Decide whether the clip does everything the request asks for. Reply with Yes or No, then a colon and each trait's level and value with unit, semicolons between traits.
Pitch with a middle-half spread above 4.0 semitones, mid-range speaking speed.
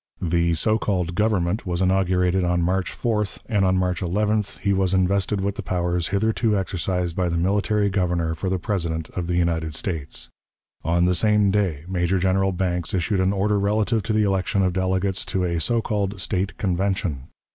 No: narrow, 2.5 semitones; average, 185 wpm